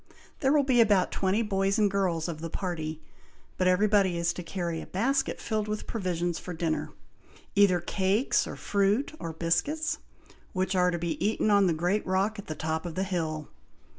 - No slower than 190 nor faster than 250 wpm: Yes, average, 195 wpm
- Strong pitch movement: No, average, 3.5 semitones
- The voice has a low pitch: No, medium, 185 Hz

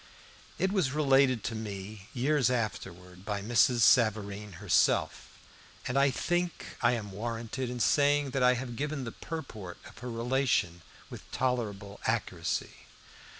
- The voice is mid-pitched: No, low, 120 Hz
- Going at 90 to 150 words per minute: Yes, average, 140 wpm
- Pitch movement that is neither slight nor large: Yes, average, 4.3 semitones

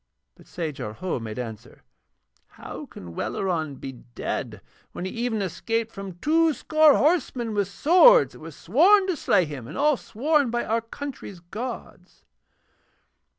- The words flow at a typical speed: Yes, average, 150 wpm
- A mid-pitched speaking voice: No, high, 225 Hz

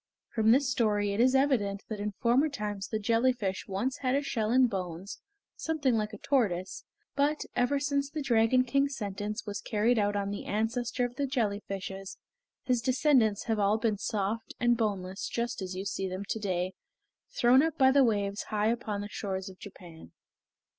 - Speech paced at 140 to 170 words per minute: No, average, 190 wpm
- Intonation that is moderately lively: Yes, average, 4.1 semitones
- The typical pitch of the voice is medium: No, high, 220 Hz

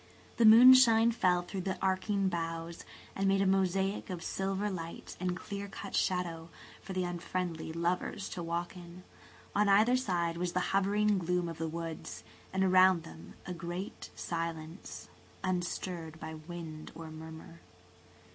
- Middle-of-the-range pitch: Yes, medium, 180 Hz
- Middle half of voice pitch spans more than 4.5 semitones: No, narrow, 2.6 semitones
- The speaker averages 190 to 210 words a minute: No, average, 155 wpm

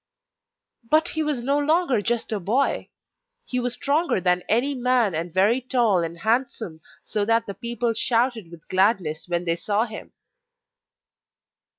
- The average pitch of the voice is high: Yes, high, 230 Hz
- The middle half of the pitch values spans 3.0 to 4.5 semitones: No, average, 5.1 semitones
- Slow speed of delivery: No, average, 155 wpm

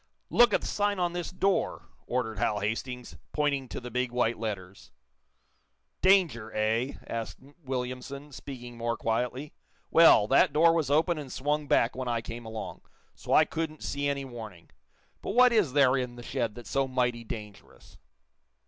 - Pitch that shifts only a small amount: No, average, 4.3 semitones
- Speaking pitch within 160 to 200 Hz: No, low, 125 Hz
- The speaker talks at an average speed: Yes, average, 165 wpm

